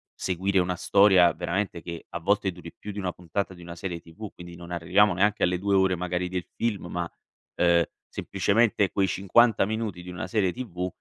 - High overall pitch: No, very low, 90 Hz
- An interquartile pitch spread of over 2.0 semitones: Yes, narrow, 2.4 semitones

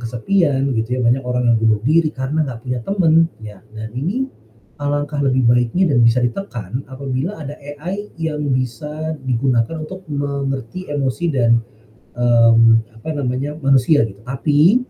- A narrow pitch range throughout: No, average, 4.1 semitones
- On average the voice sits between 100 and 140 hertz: Yes, low, 135 Hz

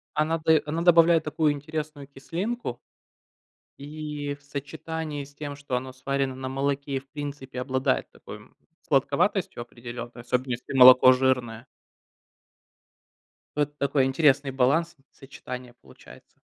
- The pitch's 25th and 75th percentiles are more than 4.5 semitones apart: No, average, 2.7 semitones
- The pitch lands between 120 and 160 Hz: Yes, medium, 140 Hz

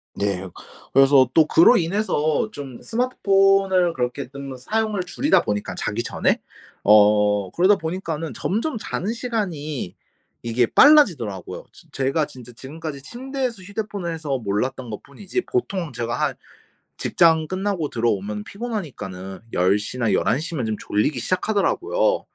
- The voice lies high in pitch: No, medium, 155 Hz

